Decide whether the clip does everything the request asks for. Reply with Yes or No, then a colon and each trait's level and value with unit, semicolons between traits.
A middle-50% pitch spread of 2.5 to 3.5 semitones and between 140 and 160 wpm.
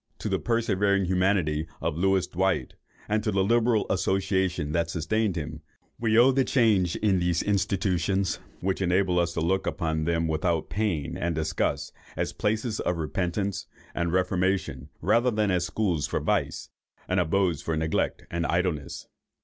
Yes: average, 3.0 semitones; average, 155 wpm